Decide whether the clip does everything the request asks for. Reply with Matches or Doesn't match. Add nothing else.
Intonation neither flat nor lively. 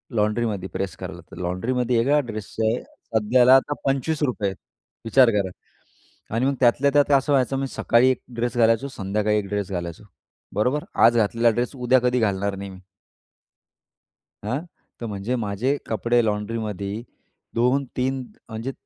Matches